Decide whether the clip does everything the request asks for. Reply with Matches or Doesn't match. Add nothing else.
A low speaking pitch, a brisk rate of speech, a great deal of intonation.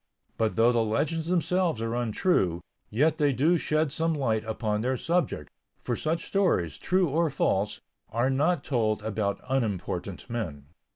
Doesn't match